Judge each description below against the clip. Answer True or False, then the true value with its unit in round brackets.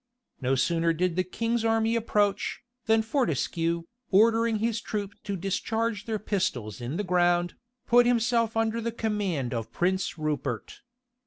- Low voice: False (205 Hz)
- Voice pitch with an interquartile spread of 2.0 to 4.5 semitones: False (4.9 semitones)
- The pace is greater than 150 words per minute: False (145 wpm)